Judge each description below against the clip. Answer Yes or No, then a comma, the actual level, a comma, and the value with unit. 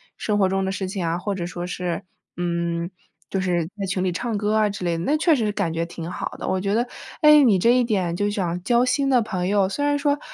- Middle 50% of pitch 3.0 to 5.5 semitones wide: Yes, average, 4.4 semitones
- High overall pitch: Yes, high, 195 Hz